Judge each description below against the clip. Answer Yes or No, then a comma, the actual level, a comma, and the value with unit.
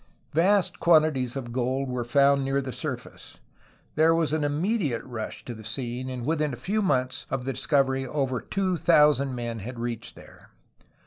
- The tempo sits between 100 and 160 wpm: No, average, 175 wpm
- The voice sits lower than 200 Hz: Yes, low, 135 Hz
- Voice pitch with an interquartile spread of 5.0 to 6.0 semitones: No, average, 3.7 semitones